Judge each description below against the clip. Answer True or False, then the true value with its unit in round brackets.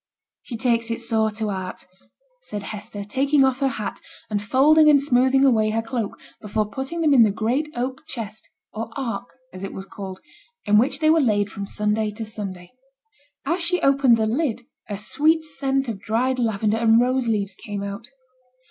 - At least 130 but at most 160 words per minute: False (185 wpm)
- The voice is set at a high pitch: True (230 Hz)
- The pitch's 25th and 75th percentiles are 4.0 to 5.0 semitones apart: True (4.3 semitones)